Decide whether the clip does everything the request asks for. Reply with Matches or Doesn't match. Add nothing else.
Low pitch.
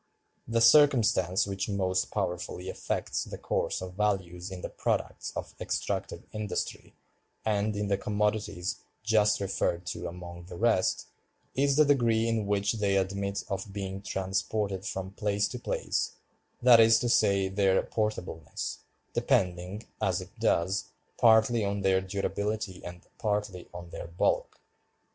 Matches